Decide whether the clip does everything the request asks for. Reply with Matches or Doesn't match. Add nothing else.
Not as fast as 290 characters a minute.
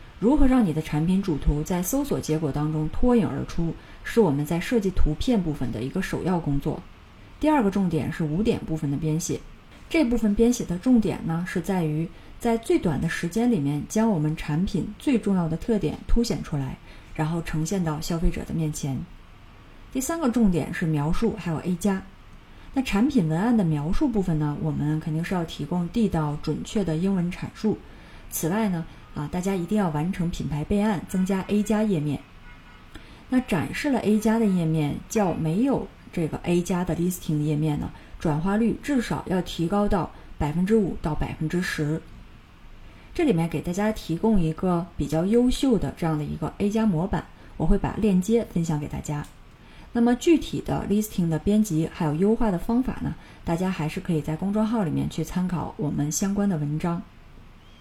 Doesn't match